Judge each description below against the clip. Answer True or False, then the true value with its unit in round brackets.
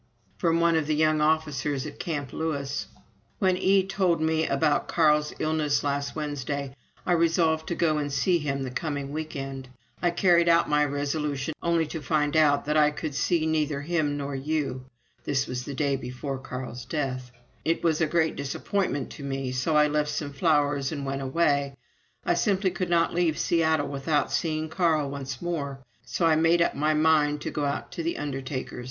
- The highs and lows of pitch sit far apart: False (2.5 semitones)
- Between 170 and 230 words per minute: True (185 wpm)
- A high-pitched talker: False (150 Hz)